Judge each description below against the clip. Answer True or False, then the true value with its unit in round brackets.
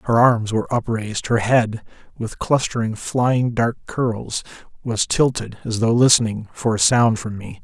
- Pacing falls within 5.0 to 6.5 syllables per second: False (4.4 syllables/s)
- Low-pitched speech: True (115 Hz)